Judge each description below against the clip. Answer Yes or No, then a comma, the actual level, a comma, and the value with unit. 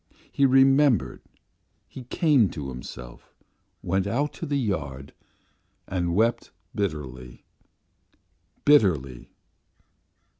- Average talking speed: No, slow, 85 wpm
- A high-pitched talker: No, very low, 95 Hz